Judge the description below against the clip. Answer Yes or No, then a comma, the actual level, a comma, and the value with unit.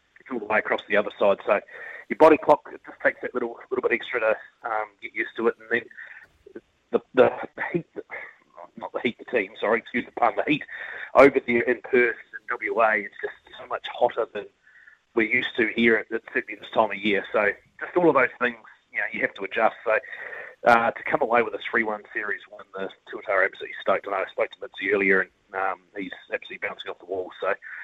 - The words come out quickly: Yes, fast, 230 wpm